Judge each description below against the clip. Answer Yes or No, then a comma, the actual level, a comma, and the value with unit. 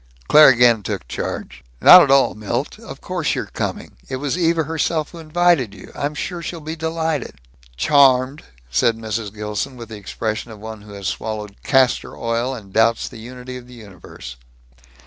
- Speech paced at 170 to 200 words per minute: Yes, average, 180 wpm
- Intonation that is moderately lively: No, wide, 5.7 semitones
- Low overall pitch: Yes, low, 125 Hz